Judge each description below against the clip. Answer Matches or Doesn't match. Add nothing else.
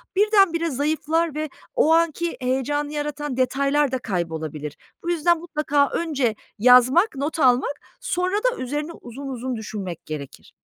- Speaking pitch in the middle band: Doesn't match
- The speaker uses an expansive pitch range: Doesn't match